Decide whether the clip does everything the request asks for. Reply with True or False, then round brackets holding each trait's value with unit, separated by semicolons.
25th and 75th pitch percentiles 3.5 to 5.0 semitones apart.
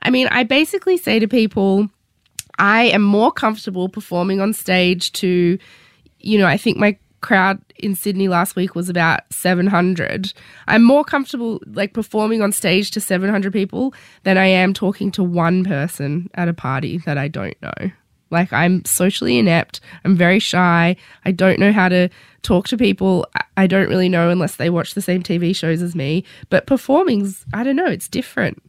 False (3.0 semitones)